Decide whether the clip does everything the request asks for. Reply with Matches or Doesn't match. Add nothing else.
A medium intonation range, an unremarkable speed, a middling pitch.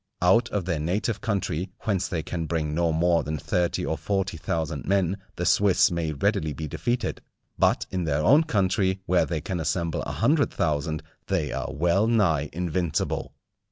Doesn't match